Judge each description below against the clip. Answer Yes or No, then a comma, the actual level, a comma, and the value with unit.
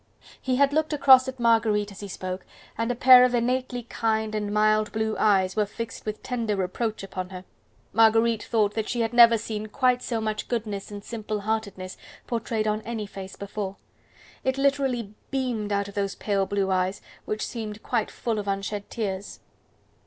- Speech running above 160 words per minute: Yes, average, 180 wpm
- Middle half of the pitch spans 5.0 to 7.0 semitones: No, average, 2.7 semitones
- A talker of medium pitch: No, high, 215 Hz